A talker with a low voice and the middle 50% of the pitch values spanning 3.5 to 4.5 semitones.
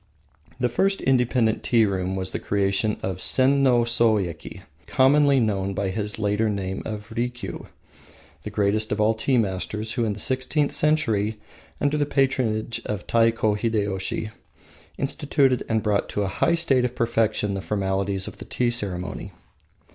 Yes: low, 110 Hz; average, 3.8 semitones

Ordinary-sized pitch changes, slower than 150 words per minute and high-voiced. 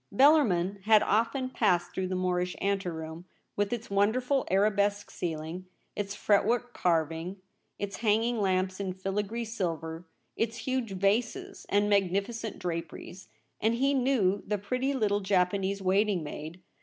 Yes: average, 3.4 semitones; average, 140 wpm; high, 200 Hz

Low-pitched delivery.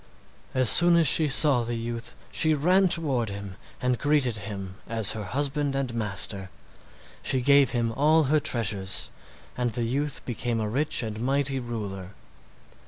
Yes: low, 120 Hz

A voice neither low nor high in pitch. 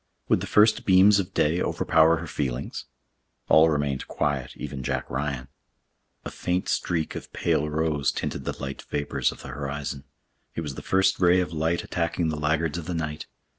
No: very low, 80 Hz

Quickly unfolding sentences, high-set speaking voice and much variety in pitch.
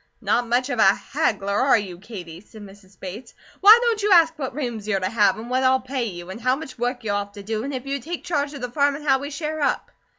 Yes: fast, 270 wpm; high, 245 Hz; wide, 5.7 semitones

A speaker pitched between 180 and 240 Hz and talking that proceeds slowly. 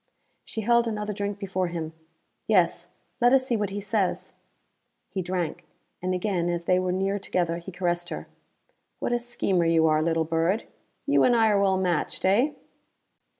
No: high, 190 Hz; average, 175 wpm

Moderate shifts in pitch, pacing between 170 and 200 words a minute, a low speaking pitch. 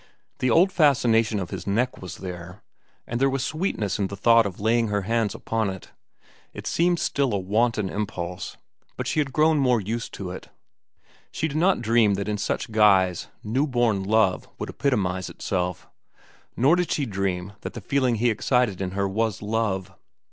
Yes: average, 4.5 semitones; average, 185 wpm; low, 110 Hz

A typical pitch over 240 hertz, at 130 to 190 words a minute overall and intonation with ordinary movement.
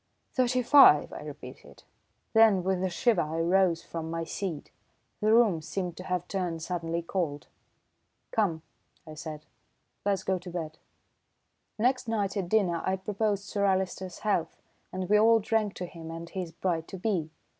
No: medium, 185 Hz; average, 165 wpm; average, 3.8 semitones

